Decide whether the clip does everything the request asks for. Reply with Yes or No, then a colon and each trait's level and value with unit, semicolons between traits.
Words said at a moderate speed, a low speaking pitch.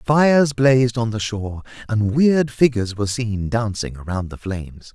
Yes: average, 170 wpm; low, 115 Hz